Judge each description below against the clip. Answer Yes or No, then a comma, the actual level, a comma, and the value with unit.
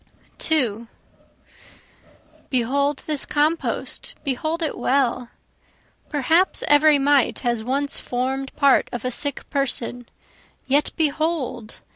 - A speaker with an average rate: No, slow, 100 wpm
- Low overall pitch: No, very high, 275 Hz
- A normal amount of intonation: Yes, average, 3.0 semitones